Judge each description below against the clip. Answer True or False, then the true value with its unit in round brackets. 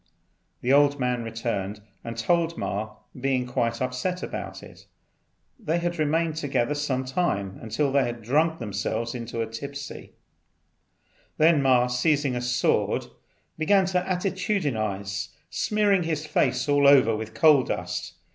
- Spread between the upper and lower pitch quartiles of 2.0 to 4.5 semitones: False (5.3 semitones)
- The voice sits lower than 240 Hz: True (135 Hz)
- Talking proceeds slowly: True (130 wpm)